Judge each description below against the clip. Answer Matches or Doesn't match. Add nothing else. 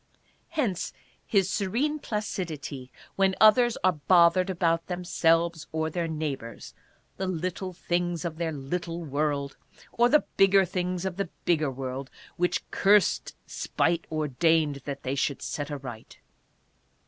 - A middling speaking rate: Doesn't match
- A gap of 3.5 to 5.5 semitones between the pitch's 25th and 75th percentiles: Matches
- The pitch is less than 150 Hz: Doesn't match